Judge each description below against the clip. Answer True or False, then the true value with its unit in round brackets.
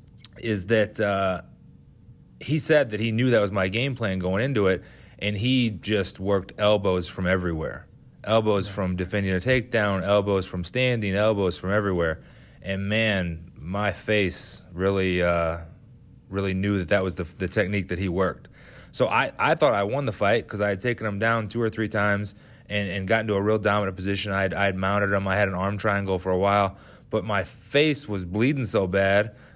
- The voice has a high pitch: False (100 Hz)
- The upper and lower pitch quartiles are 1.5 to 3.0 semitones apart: True (2.6 semitones)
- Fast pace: False (195 wpm)